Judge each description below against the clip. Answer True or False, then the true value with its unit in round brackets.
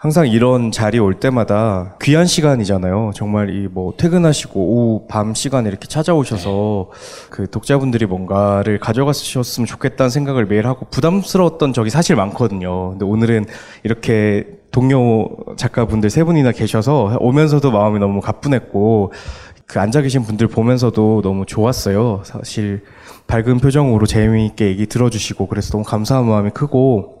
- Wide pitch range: False (4.3 semitones)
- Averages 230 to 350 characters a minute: False (360 characters per minute)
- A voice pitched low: True (110 Hz)